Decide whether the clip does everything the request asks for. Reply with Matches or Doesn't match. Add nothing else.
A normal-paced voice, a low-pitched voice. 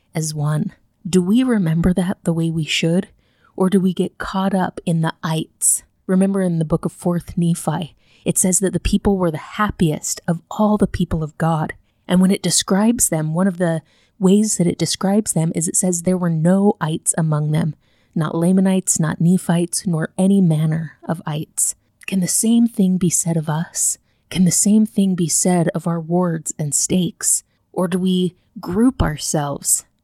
Doesn't match